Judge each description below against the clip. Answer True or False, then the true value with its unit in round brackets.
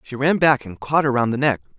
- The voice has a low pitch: True (130 Hz)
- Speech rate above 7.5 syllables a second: False (5.8 syllables/s)